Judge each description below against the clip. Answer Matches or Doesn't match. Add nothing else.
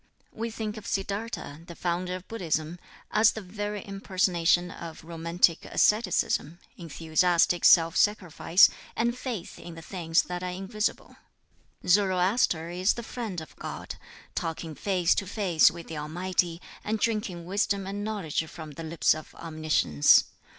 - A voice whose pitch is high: Doesn't match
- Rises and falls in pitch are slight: Doesn't match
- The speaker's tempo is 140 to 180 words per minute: Matches